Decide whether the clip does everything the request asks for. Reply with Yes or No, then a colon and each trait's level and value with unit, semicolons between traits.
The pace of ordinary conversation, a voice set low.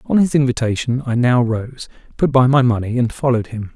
No: fast, 210 wpm; low, 125 Hz